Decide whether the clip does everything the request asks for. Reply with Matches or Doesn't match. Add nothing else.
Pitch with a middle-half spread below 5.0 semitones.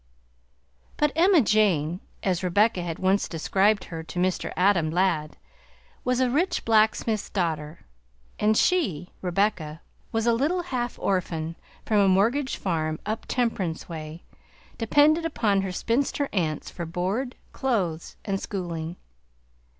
Doesn't match